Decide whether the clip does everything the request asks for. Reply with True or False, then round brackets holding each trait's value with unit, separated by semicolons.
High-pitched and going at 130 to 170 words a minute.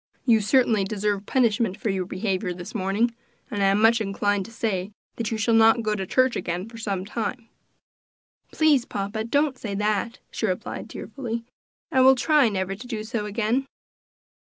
False (220 Hz; 180 wpm)